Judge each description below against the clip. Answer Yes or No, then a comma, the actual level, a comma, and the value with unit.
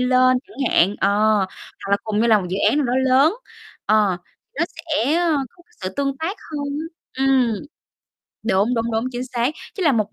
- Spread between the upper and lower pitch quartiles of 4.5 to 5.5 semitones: Yes, average, 4.9 semitones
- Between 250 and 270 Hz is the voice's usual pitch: Yes, very high, 255 Hz